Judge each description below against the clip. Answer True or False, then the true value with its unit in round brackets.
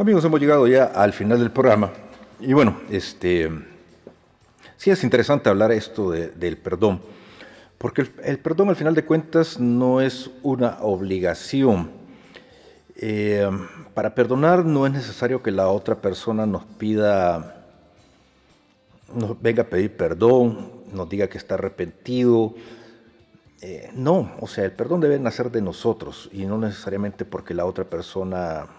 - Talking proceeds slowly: False (145 wpm)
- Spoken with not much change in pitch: False (4.7 semitones)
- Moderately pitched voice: False (115 Hz)